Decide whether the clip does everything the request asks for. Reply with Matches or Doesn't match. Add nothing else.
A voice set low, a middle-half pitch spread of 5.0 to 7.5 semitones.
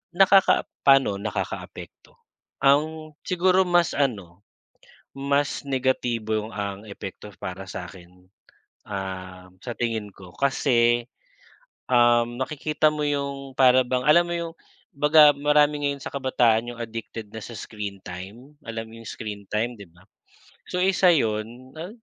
Matches